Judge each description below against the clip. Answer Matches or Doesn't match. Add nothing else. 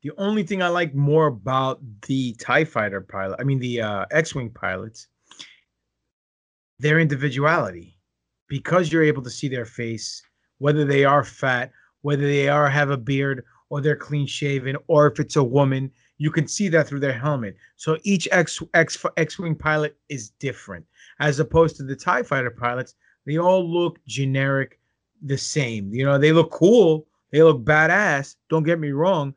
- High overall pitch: Doesn't match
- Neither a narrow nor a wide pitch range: Matches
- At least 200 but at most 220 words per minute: Doesn't match